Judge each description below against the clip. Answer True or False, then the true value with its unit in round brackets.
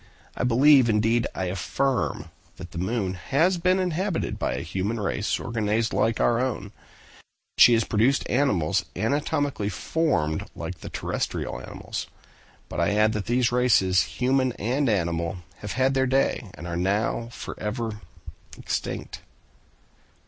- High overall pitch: False (115 Hz)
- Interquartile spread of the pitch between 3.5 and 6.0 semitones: True (5.1 semitones)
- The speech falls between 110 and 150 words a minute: True (140 wpm)